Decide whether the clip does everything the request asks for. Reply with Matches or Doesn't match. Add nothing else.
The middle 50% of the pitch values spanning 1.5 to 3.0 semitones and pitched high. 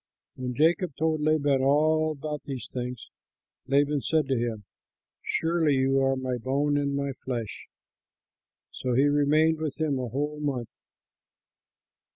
Doesn't match